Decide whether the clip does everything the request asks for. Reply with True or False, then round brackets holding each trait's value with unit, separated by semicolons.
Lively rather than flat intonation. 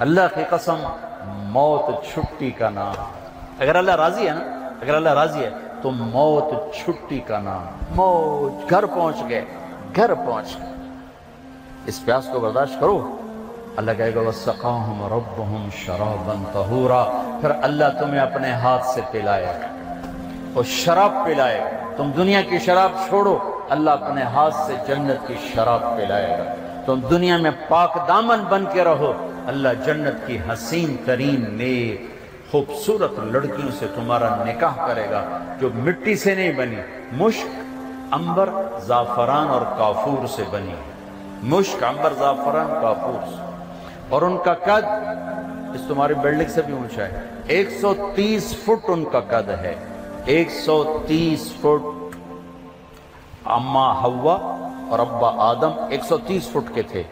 True (7.7 semitones)